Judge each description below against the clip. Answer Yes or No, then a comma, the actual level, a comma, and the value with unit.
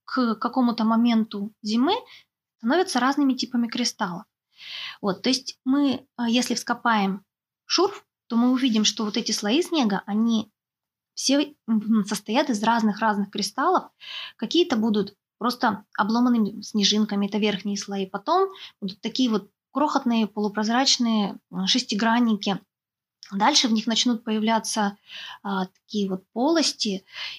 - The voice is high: Yes, high, 225 Hz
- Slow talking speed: No, average, 120 wpm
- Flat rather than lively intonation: No, average, 3.8 semitones